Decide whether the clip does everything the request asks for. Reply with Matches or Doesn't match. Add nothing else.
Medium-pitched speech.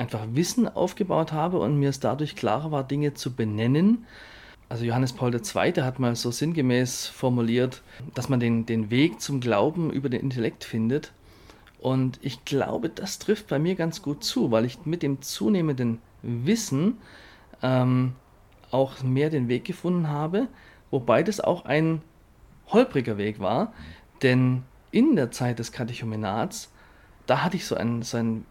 Doesn't match